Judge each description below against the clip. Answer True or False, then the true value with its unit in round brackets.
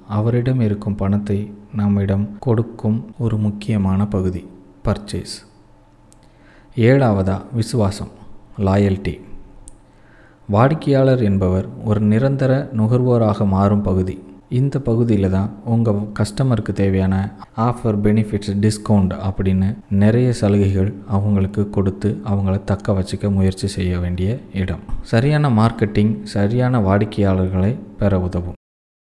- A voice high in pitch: False (105 Hz)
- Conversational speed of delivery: True (95 wpm)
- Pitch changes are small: True (2.3 semitones)